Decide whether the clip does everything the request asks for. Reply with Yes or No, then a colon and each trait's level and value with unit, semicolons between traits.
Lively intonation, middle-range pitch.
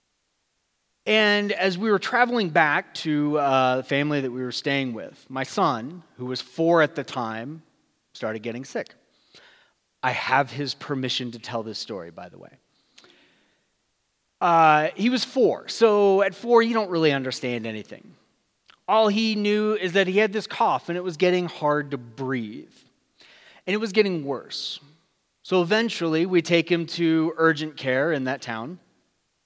Yes: wide, 7.0 semitones; medium, 160 Hz